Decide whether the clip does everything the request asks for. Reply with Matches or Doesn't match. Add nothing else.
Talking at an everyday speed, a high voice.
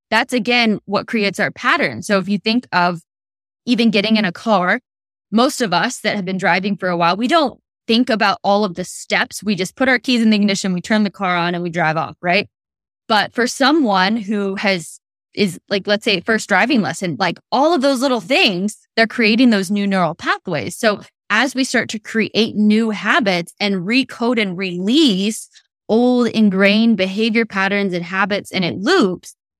Matches